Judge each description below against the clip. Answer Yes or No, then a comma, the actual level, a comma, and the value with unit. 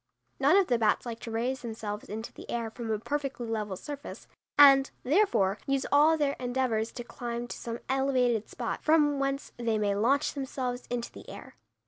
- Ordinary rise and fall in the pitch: Yes, average, 3.5 semitones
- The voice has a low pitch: No, high, 245 Hz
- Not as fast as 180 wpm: No, average, 185 wpm